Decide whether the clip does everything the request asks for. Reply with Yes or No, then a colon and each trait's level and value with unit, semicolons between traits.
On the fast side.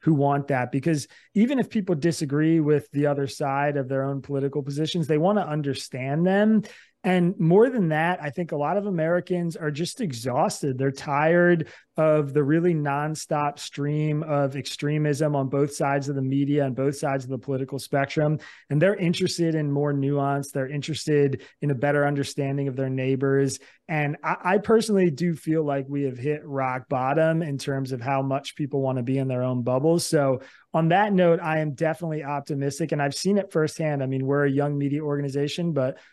No: average, 195 wpm